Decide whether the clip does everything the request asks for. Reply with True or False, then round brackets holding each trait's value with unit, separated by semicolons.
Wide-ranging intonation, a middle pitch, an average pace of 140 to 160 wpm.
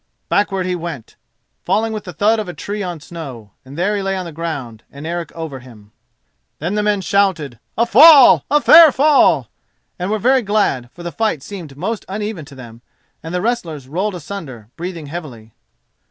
False (6.4 semitones; 175 Hz; 185 wpm)